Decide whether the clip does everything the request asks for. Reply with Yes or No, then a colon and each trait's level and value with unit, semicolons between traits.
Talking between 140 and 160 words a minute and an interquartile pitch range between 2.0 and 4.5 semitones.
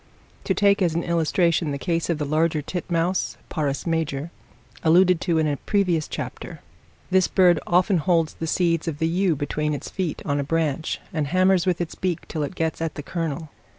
No: average, 195 wpm; narrow, 2.5 semitones